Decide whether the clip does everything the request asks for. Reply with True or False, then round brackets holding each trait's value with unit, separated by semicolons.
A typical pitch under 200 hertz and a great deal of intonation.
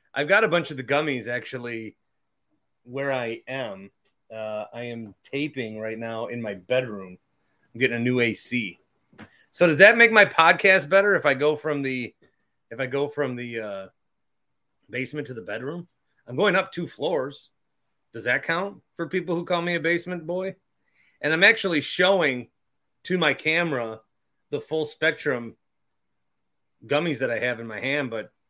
True (140 Hz; 6.2 semitones)